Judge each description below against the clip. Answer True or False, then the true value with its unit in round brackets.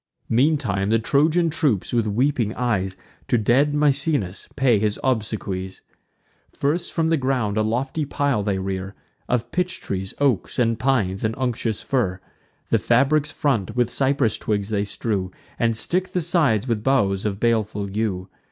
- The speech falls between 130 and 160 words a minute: True (155 wpm)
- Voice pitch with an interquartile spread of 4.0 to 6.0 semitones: True (5.2 semitones)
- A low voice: True (115 Hz)